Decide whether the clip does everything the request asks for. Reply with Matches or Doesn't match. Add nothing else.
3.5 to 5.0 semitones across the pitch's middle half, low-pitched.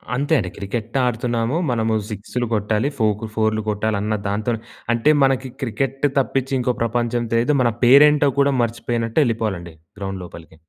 Doesn't match